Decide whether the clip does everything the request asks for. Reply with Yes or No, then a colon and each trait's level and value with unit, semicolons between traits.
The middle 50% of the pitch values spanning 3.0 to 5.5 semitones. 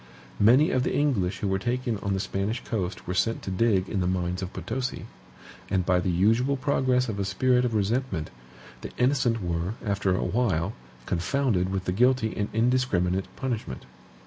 Yes: average, 5.1 semitones